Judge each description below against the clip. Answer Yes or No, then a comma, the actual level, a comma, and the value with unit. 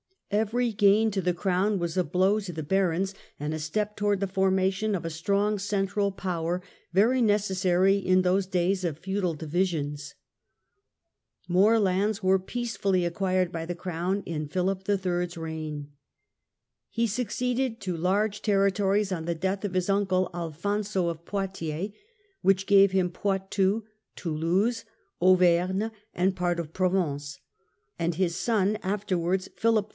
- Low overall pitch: No, high, 190 Hz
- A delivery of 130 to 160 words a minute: Yes, average, 150 wpm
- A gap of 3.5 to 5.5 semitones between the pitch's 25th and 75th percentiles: No, narrow, 2.5 semitones